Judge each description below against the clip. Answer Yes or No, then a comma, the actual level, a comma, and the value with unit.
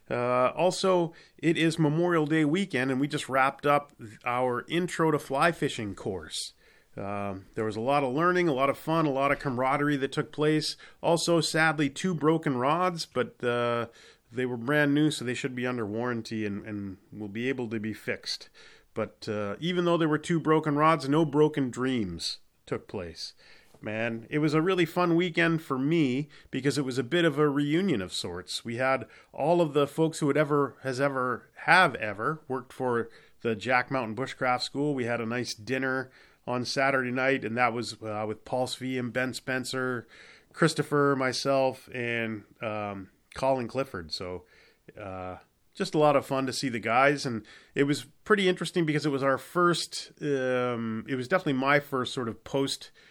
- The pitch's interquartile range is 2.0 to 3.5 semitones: No, average, 4.1 semitones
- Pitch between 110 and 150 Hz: Yes, low, 135 Hz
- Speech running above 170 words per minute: Yes, average, 190 wpm